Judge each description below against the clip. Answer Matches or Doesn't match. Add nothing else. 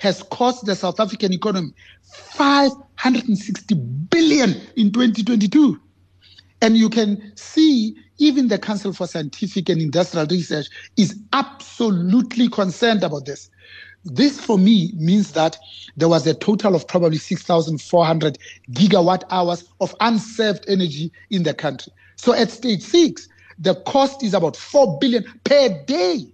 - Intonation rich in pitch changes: Matches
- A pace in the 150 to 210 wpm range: Doesn't match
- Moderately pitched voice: Doesn't match